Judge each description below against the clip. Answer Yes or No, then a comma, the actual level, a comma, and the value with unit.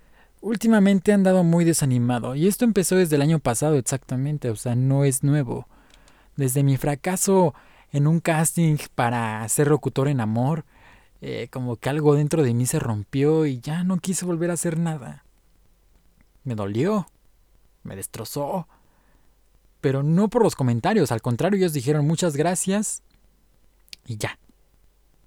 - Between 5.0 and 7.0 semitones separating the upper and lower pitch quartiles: Yes, average, 5.3 semitones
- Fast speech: No, average, 150 wpm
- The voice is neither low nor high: Yes, medium, 150 Hz